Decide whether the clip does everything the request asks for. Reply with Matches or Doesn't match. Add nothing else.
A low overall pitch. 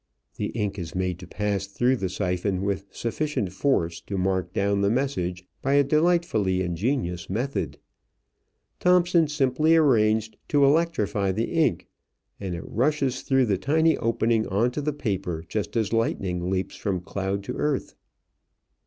Matches